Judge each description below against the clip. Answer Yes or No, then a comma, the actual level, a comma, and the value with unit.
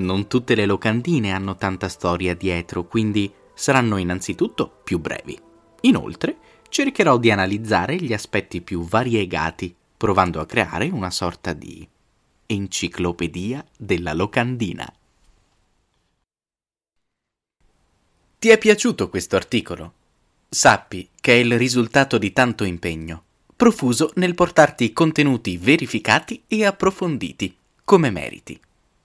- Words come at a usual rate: No, slow, 105 wpm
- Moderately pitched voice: No, low, 110 Hz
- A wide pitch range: Yes, wide, 7.3 semitones